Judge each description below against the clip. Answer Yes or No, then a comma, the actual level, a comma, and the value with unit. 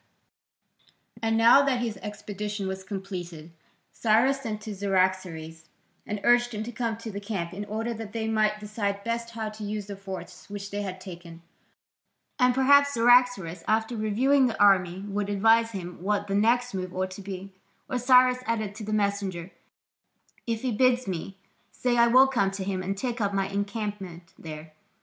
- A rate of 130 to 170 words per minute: No, average, 180 wpm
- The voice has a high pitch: Yes, high, 210 Hz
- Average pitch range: Yes, average, 3.2 semitones